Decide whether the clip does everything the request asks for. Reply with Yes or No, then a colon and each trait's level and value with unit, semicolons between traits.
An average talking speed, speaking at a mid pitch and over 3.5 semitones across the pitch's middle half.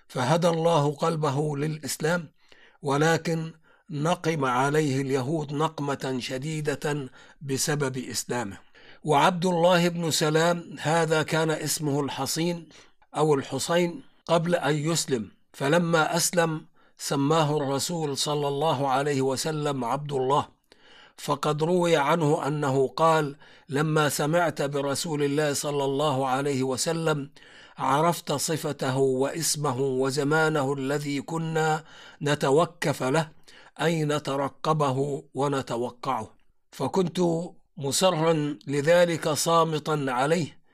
No: average, 95 wpm; medium, 150 Hz; average, 2.9 semitones